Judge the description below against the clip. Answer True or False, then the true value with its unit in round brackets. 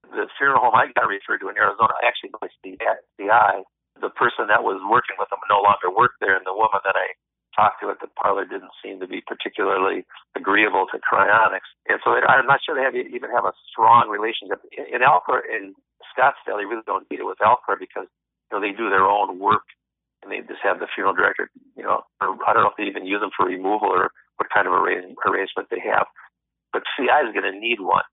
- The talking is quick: True (235 wpm)